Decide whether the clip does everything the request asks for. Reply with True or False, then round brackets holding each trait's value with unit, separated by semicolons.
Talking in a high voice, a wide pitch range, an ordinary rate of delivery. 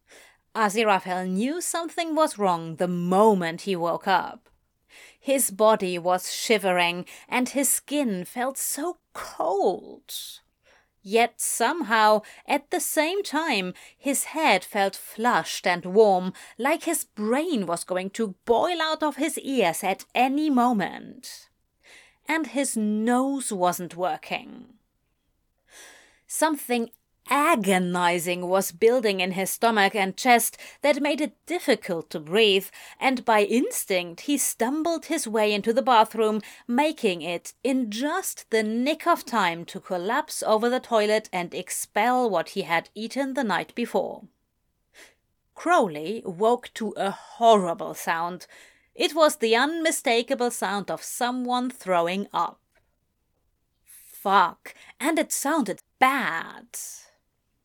False (225 Hz; 6.4 semitones; 125 wpm)